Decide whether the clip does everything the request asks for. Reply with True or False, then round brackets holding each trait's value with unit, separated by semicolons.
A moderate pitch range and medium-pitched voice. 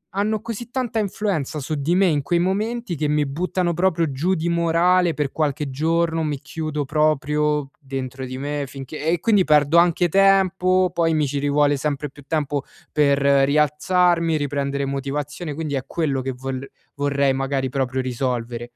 True (3.7 semitones; 150 Hz)